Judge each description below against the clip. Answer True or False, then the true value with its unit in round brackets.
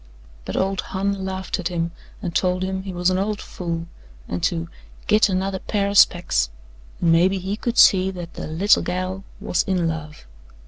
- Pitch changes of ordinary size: False (2.0 semitones)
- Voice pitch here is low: False (185 Hz)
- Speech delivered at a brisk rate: False (185 wpm)